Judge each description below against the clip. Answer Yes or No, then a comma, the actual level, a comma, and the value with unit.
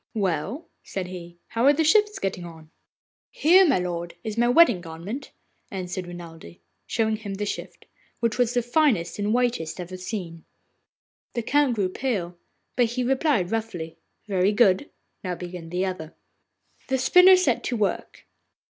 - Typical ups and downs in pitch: No, wide, 5.8 semitones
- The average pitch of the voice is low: No, high, 205 Hz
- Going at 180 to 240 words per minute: No, average, 155 wpm